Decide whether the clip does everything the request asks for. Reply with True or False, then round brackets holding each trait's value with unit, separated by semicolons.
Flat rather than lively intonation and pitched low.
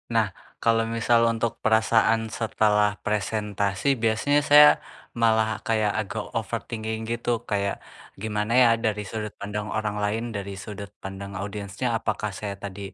True (1.7 semitones; 110 Hz)